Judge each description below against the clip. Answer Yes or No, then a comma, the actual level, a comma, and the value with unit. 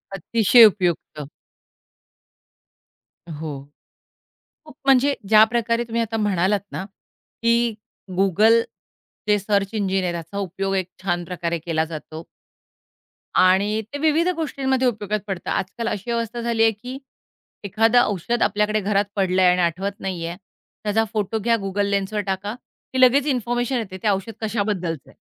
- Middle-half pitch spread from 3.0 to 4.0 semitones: Yes, average, 3.7 semitones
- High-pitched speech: Yes, high, 205 Hz